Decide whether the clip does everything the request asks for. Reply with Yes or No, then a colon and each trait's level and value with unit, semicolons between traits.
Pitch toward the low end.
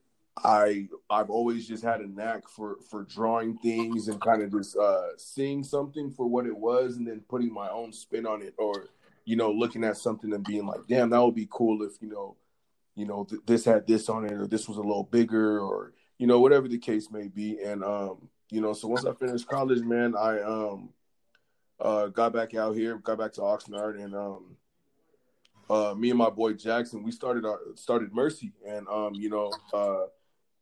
Yes: low, 110 Hz